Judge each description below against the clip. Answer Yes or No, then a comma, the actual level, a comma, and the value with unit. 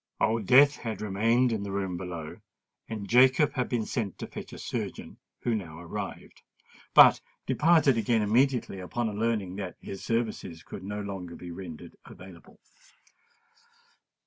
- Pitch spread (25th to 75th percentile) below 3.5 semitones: No, average, 4.2 semitones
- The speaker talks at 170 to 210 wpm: No, average, 145 wpm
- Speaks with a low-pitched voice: Yes, low, 105 Hz